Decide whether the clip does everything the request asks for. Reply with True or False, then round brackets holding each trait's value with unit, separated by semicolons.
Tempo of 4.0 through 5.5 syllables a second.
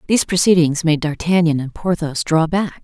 True (5.3 syllables/s)